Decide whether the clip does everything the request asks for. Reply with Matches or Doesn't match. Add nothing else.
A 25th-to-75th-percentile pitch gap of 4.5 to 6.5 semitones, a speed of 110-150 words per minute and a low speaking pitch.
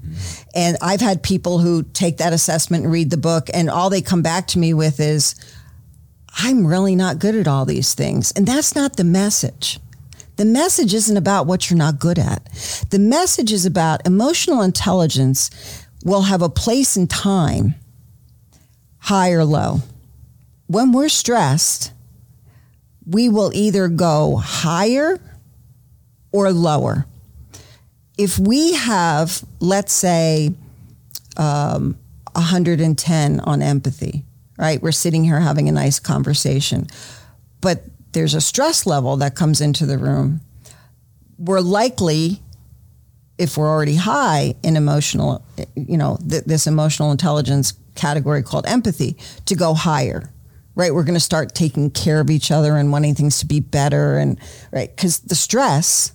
Doesn't match